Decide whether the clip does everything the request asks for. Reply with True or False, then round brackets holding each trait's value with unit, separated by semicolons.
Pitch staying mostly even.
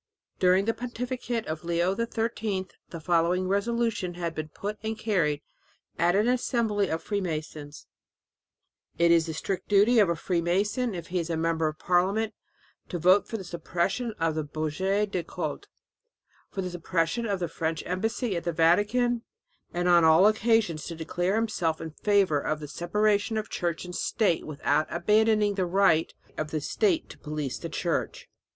False (4.3 semitones)